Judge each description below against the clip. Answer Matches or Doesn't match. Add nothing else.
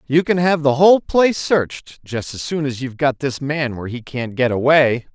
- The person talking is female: Doesn't match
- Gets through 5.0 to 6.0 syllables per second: Matches